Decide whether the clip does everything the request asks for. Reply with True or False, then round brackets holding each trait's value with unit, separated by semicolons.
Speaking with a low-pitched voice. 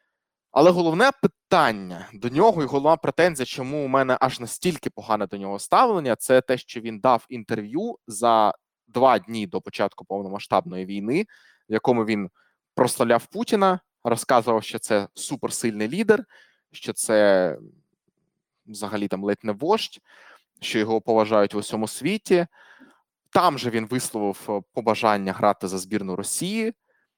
True (115 Hz)